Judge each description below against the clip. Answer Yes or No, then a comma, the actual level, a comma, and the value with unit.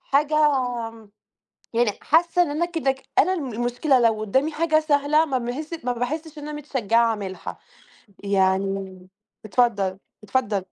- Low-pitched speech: No, very high, 250 Hz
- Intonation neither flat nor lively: No, wide, 5.9 semitones